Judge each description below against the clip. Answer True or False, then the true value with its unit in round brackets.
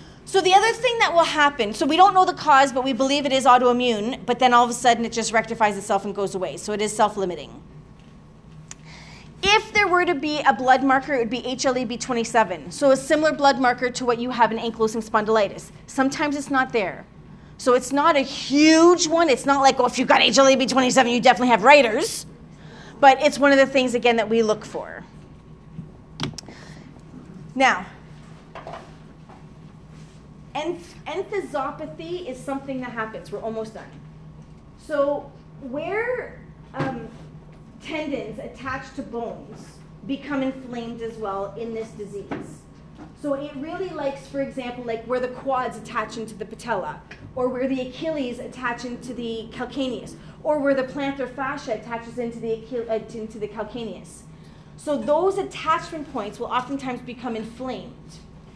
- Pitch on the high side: True (255 Hz)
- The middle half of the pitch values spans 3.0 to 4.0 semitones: True (3.7 semitones)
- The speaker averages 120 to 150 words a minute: False (165 wpm)